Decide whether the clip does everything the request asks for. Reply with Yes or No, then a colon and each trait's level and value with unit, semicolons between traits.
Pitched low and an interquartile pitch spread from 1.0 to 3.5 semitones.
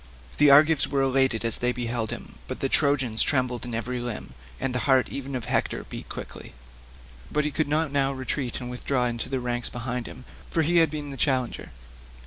Yes: low, 130 Hz; narrow, 2.6 semitones